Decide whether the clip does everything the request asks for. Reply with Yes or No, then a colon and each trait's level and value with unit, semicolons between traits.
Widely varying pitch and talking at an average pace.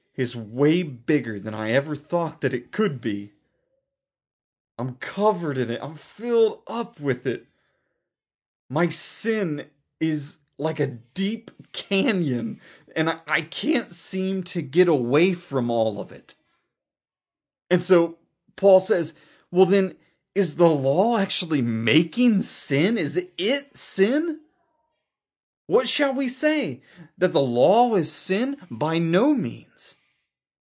No: wide, 6.9 semitones; slow, 130 wpm